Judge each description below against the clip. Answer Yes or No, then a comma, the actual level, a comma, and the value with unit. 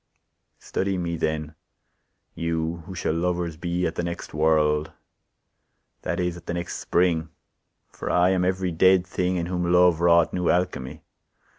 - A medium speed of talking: Yes, average, 155 wpm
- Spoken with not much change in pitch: Yes, narrow, 1.7 semitones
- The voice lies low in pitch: Yes, very low, 85 Hz